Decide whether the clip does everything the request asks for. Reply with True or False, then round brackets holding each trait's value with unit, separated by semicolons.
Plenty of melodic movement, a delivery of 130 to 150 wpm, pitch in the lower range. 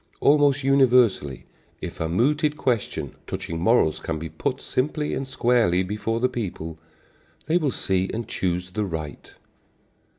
True (7.2 semitones; 140 wpm; 115 Hz)